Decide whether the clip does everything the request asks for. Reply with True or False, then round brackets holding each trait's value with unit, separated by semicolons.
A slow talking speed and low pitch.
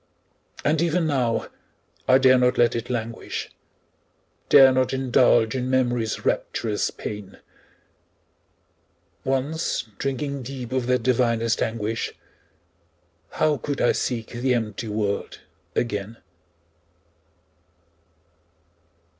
True (95 wpm; 125 Hz)